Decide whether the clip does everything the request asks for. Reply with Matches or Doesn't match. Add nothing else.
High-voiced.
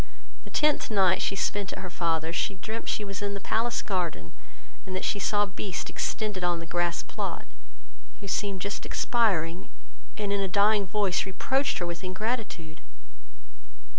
Matches